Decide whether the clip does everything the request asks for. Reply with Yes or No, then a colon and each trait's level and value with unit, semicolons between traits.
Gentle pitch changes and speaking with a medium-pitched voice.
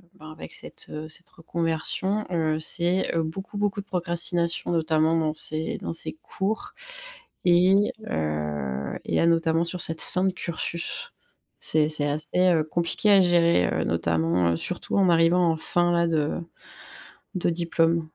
Yes: narrow, 2.1 semitones; medium, 165 Hz